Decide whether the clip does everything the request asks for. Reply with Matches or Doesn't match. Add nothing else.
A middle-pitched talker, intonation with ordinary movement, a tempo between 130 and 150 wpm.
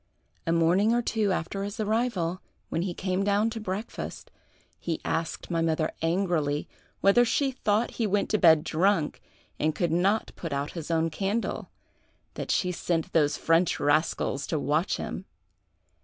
Doesn't match